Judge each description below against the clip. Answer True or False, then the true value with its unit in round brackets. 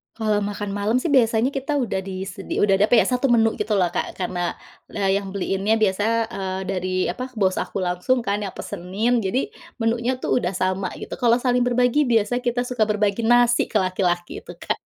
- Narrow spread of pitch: False (4.0 semitones)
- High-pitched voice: True (210 Hz)